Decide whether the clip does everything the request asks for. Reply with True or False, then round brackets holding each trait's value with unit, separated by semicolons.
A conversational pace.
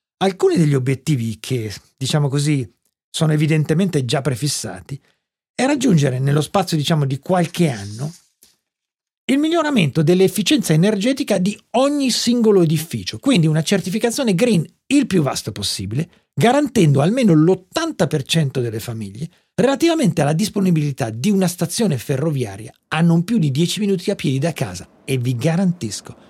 True (135 wpm)